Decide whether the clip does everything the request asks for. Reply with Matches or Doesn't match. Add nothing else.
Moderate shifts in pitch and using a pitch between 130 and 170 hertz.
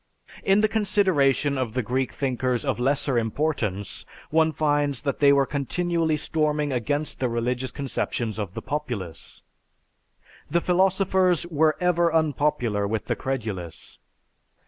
Matches